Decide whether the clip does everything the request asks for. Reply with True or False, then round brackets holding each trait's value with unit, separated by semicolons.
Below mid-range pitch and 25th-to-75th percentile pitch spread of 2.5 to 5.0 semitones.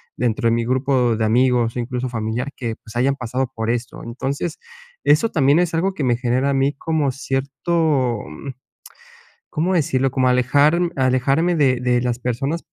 True (130 Hz; 2.8 semitones)